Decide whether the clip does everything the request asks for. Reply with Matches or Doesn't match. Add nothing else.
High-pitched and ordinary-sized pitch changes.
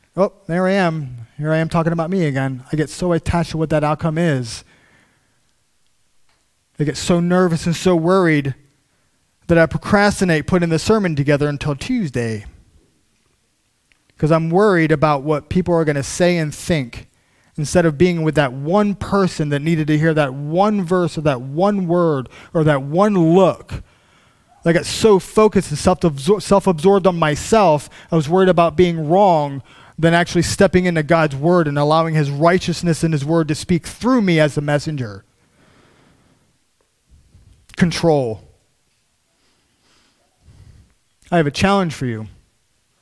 Doesn't match